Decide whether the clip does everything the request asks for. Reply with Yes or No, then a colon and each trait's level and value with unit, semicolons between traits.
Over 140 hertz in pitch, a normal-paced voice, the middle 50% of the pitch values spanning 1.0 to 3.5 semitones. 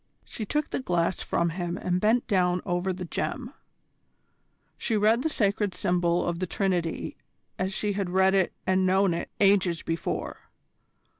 Yes: medium, 185 Hz; average, 160 wpm; narrow, 2.4 semitones